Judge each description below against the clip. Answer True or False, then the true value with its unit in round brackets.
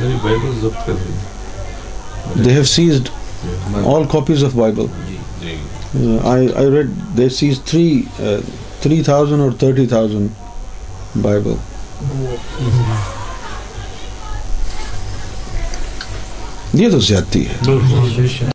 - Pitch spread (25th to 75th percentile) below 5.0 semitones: False (5.4 semitones)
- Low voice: True (110 Hz)